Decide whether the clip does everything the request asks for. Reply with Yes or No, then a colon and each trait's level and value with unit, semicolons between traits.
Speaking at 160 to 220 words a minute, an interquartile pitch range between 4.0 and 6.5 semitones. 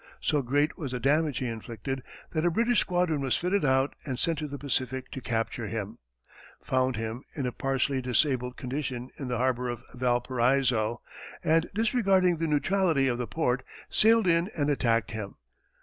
Yes: average, 175 wpm; average, 4.3 semitones